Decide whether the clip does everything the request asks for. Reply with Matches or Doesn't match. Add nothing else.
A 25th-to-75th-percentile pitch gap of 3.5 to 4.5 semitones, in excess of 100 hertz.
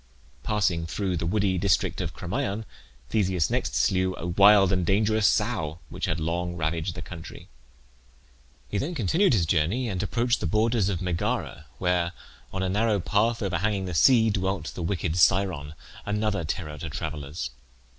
Doesn't match